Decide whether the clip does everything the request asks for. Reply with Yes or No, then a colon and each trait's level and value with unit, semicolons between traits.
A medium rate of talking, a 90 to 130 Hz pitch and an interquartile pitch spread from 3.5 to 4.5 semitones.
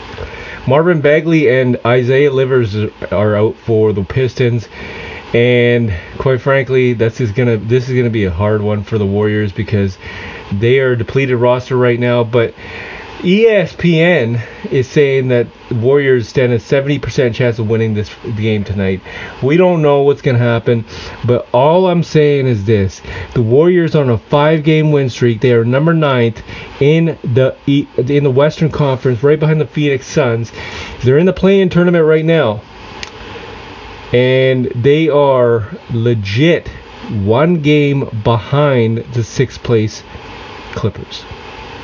Yes: average, 155 wpm; low, 125 Hz; average, 4.2 semitones